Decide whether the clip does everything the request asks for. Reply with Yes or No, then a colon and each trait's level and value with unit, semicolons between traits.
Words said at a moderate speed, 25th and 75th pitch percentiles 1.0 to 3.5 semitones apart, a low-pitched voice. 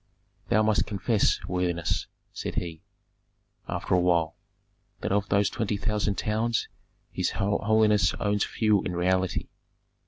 No: slow, 125 wpm; average, 2.9 semitones; low, 100 Hz